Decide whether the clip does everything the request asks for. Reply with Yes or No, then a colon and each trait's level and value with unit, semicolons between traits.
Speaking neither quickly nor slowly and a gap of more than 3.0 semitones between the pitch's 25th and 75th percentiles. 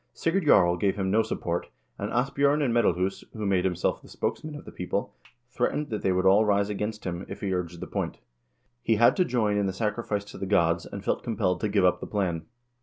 No: fast, 235 wpm; average, 3.6 semitones